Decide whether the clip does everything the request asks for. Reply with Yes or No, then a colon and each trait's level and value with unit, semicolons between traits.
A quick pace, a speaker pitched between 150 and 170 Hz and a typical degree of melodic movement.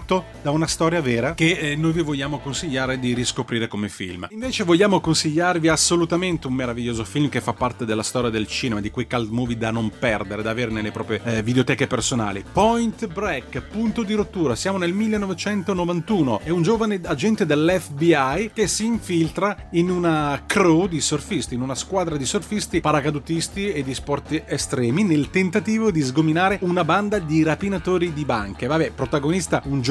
No: fast, 175 wpm; medium, 160 Hz; wide, 6.6 semitones